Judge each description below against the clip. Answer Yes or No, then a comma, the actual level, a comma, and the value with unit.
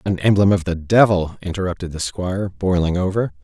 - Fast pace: No, average, 175 wpm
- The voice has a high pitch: No, very low, 90 Hz